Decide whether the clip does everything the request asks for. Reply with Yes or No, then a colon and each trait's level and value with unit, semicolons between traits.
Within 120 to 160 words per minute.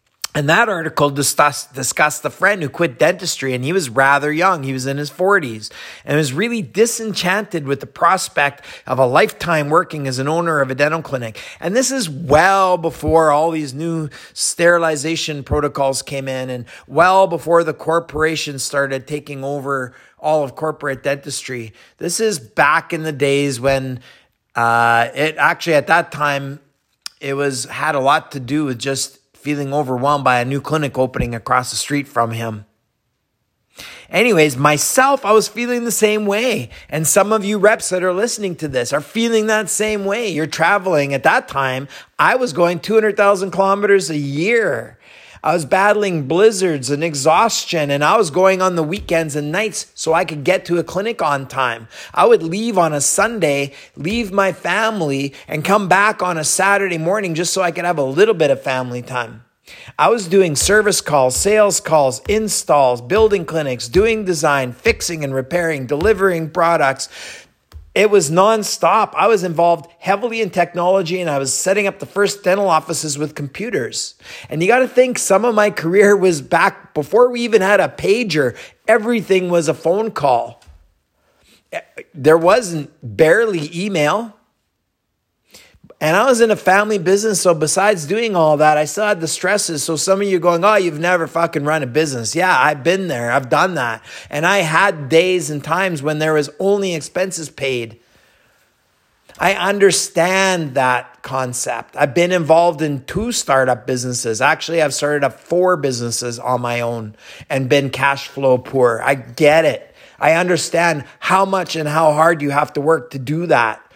No: average, 175 wpm